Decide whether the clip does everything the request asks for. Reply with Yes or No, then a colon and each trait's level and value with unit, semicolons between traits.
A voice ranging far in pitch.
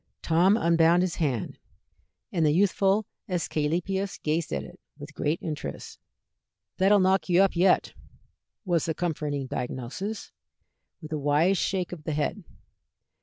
No: average, 3.9 semitones